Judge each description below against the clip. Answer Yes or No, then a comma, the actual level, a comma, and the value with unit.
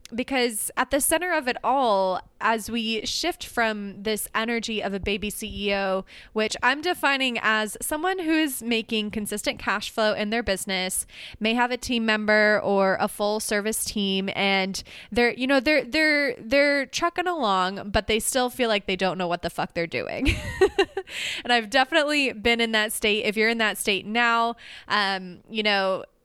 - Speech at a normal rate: Yes, average, 180 wpm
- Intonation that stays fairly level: No, average, 3.6 semitones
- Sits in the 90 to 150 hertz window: No, high, 220 Hz